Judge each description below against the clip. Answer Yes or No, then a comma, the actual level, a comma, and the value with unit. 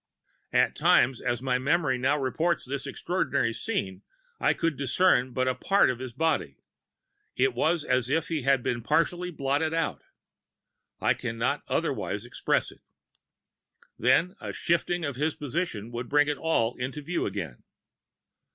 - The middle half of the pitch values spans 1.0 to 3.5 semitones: No, average, 4.7 semitones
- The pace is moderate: Yes, average, 155 wpm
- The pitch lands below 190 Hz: Yes, low, 135 Hz